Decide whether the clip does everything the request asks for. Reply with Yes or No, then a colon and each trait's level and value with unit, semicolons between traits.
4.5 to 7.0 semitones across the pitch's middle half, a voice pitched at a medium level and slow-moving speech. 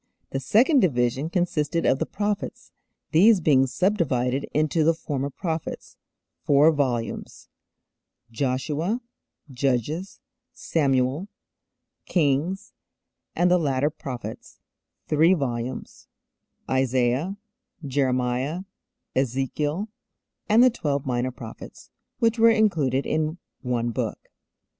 Yes: average, 5.1 semitones; medium, 145 Hz; slow, 95 wpm